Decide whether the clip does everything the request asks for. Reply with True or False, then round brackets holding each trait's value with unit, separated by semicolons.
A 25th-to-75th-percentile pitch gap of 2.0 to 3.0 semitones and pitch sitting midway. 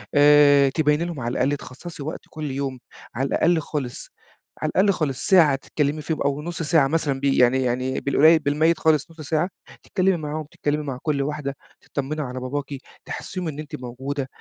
True (2.5 semitones; 145 Hz)